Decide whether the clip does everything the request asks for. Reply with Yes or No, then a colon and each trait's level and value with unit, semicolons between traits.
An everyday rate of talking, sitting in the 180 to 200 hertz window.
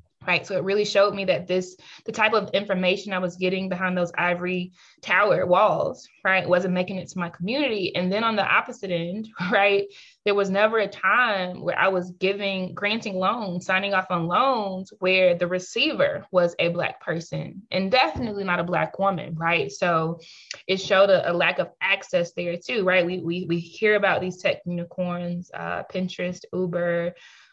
Yes: average, 185 wpm; medium, 185 Hz